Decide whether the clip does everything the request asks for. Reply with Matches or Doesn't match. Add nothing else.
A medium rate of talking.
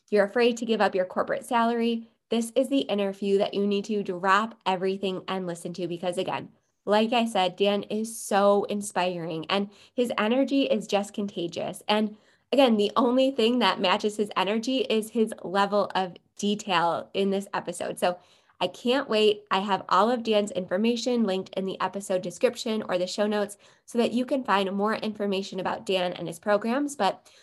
Matches